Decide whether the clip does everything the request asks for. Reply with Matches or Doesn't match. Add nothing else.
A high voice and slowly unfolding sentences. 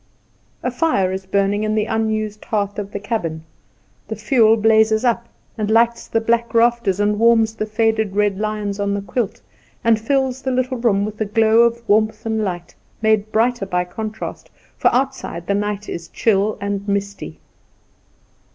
Doesn't match